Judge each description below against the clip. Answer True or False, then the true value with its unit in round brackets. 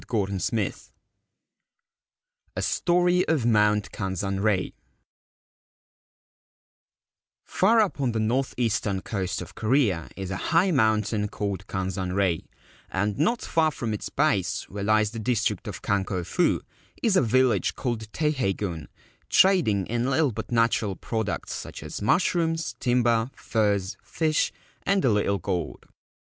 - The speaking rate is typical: False (130 wpm)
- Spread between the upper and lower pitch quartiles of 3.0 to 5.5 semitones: True (5.0 semitones)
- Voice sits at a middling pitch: False (110 Hz)